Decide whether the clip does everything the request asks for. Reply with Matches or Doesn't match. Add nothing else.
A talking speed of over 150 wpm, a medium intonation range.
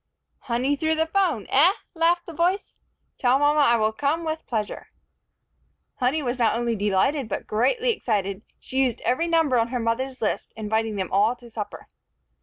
Doesn't match